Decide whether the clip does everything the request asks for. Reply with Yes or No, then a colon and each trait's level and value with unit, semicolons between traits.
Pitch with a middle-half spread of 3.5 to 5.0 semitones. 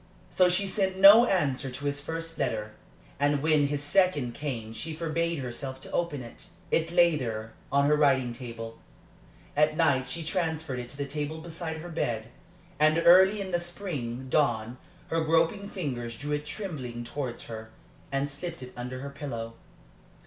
Yes: average, 4.7 semitones